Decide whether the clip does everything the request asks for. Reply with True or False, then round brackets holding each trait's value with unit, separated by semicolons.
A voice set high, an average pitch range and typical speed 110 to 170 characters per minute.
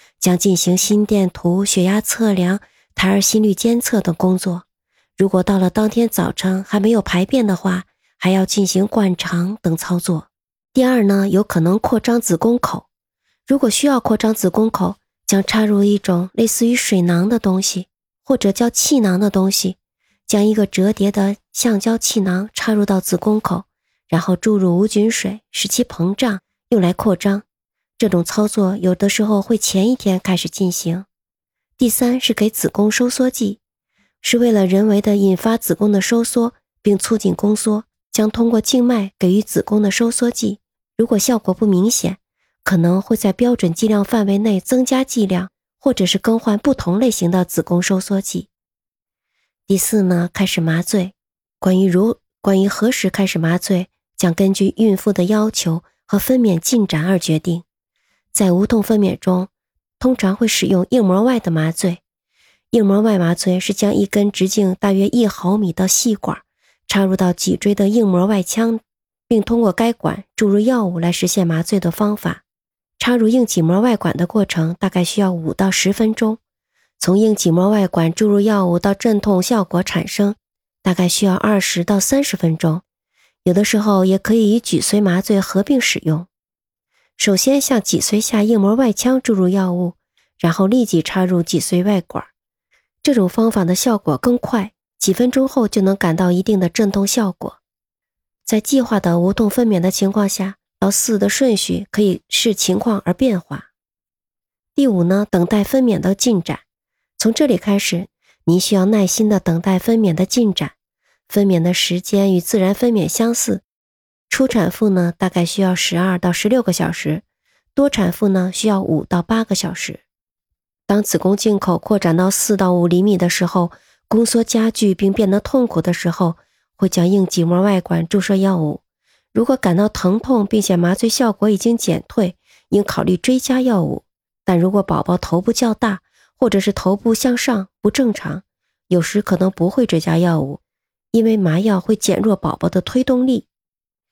False (200 Hz; 3.3 semitones; 255 characters per minute)